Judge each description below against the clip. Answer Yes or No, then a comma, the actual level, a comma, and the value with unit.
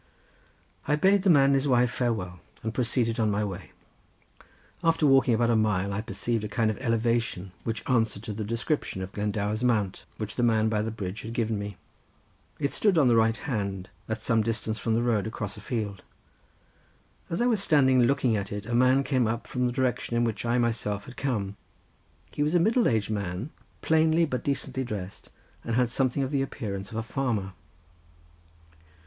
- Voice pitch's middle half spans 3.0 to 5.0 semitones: Yes, average, 3.7 semitones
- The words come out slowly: No, average, 195 wpm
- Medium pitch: No, low, 115 Hz